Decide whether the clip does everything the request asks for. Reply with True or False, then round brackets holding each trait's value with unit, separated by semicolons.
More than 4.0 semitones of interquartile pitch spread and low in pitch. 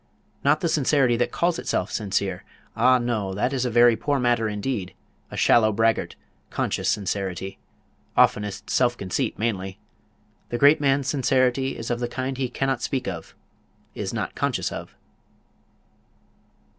True (4.4 semitones; 120 Hz)